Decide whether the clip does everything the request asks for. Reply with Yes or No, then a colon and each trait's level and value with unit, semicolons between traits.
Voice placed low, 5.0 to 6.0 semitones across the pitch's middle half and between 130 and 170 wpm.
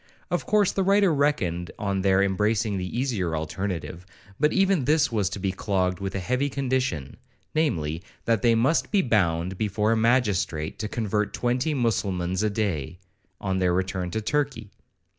Yes: low, 105 Hz; wide, 5.6 semitones; average, 160 wpm